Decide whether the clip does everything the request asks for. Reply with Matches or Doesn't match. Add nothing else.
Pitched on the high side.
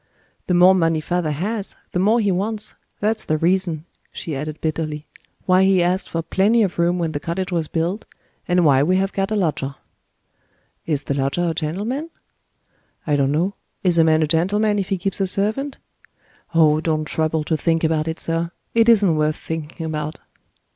Doesn't match